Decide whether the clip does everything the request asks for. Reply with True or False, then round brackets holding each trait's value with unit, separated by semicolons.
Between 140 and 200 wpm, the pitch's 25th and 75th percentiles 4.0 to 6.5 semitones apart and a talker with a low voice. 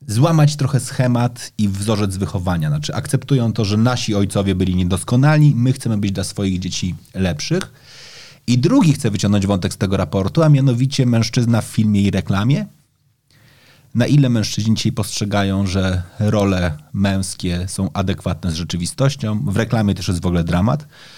True (155 wpm; 5.3 semitones; 110 Hz)